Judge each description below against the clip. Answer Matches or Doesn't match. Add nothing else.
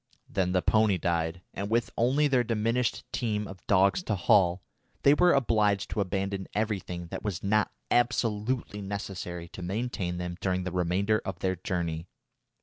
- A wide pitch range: Doesn't match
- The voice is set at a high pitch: Doesn't match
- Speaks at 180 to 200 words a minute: Doesn't match